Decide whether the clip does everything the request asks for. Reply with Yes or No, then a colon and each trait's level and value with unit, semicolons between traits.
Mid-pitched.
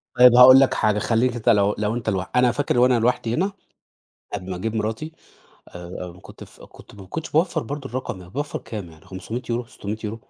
No: low, 115 Hz